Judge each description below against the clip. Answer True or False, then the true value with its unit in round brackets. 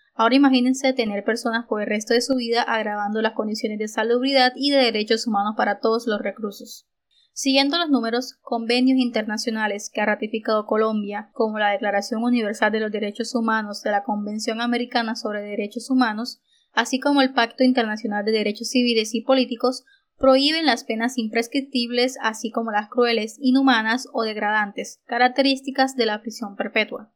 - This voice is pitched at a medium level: False (230 Hz)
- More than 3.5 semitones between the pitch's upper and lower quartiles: False (2.8 semitones)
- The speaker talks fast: False (160 wpm)